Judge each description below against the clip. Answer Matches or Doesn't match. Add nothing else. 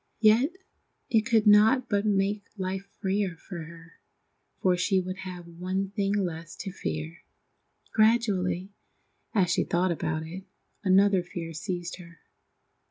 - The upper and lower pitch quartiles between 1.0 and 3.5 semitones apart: Matches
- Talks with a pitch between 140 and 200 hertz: Matches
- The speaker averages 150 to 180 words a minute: Doesn't match